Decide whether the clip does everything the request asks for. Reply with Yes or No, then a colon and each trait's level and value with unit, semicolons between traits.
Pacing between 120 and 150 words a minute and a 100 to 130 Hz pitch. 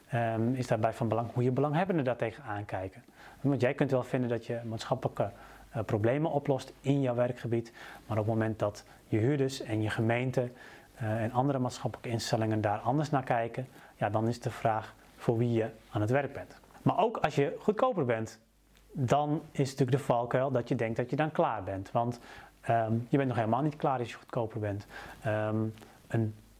No: fast, 200 wpm; low, 120 Hz